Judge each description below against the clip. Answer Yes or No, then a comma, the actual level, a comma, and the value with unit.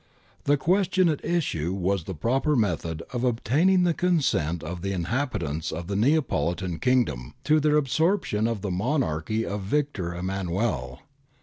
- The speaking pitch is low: Yes, low, 110 Hz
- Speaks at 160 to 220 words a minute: No, average, 150 wpm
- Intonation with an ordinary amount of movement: No, wide, 9.0 semitones